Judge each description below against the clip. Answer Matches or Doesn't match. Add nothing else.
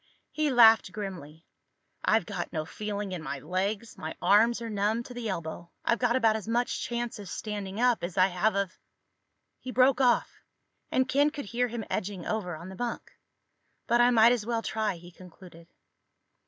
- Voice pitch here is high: Matches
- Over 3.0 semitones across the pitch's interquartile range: Matches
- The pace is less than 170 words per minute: Doesn't match